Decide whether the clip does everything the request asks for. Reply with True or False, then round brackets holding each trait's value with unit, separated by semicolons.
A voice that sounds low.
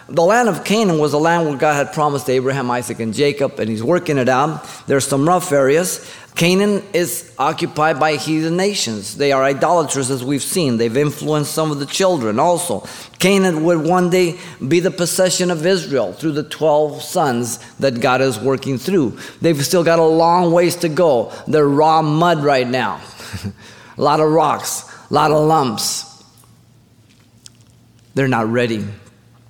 False (150 Hz)